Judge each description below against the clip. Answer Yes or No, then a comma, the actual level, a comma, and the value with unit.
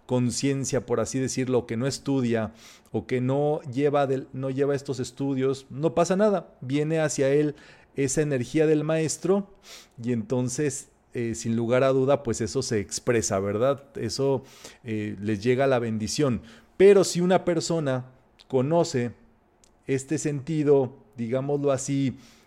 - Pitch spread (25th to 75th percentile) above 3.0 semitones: Yes, average, 3.5 semitones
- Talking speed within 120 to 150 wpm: Yes, average, 145 wpm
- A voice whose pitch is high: No, low, 135 Hz